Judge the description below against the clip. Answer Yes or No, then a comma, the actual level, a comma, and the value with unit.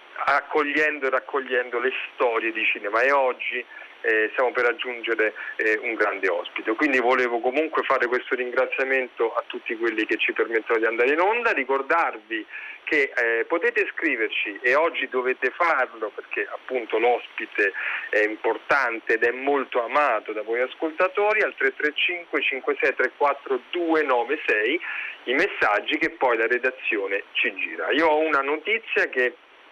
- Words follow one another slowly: No, average, 145 wpm